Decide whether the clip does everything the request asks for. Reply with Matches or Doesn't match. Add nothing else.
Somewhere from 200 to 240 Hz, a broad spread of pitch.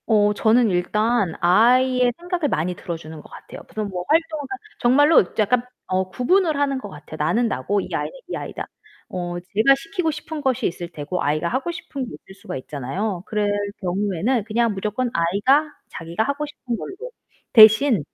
Matches